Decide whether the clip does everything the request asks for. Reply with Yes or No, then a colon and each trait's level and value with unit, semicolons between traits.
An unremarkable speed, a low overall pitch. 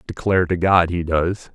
Yes: average, 195 wpm; very low, 90 Hz